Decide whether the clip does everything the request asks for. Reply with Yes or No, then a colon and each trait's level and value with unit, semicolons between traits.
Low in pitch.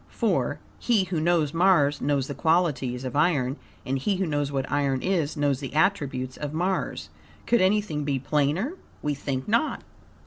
No: medium, 150 Hz